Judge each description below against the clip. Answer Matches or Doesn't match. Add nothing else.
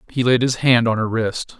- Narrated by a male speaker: Matches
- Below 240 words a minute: Doesn't match